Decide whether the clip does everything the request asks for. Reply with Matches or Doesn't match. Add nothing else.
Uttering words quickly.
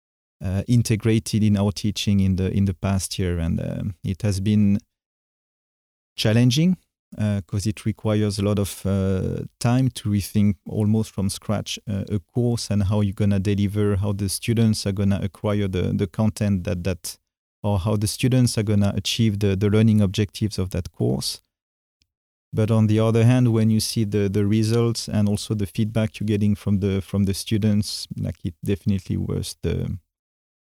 Matches